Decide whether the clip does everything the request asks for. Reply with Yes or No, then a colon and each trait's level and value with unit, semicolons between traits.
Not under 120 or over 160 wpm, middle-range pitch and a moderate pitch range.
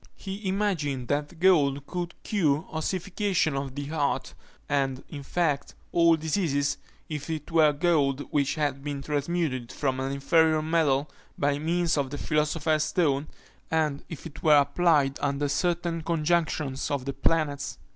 Yes: average, 145 wpm; medium, 150 Hz; average, 3.0 semitones